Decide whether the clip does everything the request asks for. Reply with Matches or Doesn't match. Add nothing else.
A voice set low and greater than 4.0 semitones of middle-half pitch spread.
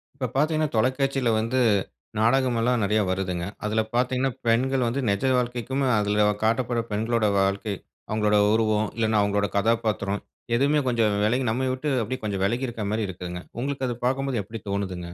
Doesn't match